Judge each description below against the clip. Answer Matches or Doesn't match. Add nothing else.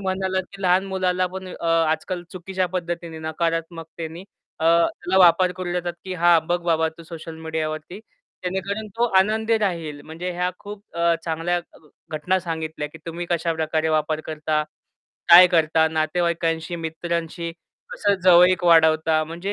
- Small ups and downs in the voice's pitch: Matches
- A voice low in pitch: Doesn't match